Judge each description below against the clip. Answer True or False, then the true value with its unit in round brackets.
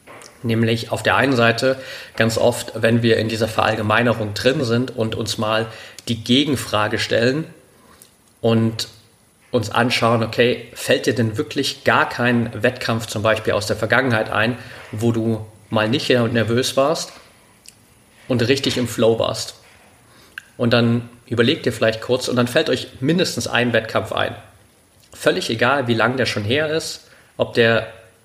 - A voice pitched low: True (115 Hz)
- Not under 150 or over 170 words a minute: True (155 wpm)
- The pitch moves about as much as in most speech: False (1.9 semitones)